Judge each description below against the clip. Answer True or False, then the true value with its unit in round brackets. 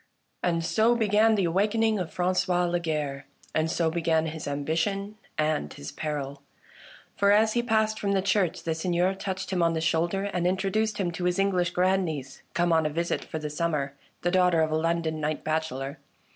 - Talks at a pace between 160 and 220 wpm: True (190 wpm)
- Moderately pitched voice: True (175 Hz)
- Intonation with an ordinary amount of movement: True (3.6 semitones)